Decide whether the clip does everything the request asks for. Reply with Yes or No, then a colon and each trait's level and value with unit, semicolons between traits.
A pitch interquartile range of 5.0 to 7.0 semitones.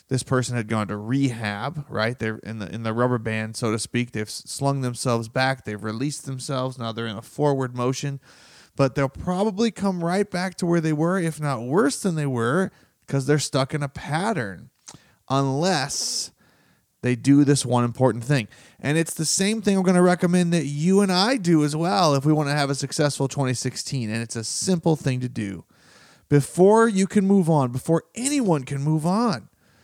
Yes: wide, 5.6 semitones